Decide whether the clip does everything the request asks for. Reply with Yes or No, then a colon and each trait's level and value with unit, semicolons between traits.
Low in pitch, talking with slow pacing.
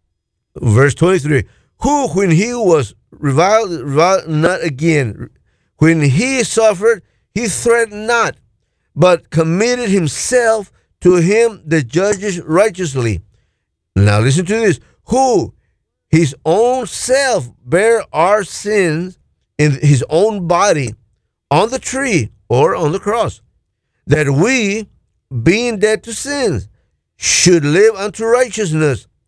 No: medium, 170 Hz; slow, 115 wpm